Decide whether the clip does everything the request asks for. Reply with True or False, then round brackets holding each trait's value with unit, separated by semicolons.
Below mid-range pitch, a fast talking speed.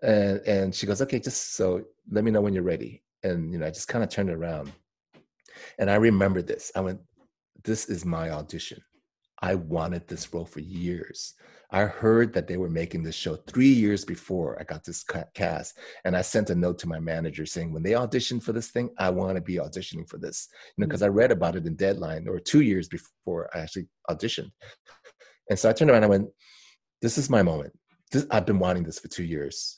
True (95 Hz; 225 wpm)